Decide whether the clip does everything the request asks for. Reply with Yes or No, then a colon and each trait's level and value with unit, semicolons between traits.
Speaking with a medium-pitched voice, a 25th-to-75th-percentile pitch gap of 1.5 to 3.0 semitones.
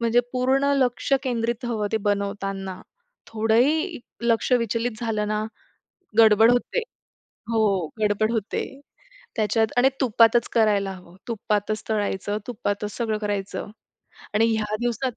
No: high, 220 Hz; narrow, 2.4 semitones